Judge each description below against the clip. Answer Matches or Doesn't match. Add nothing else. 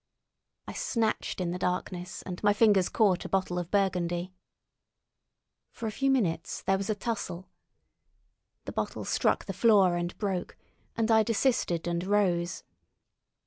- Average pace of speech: Matches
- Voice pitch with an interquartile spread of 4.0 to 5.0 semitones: Doesn't match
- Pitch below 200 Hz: Matches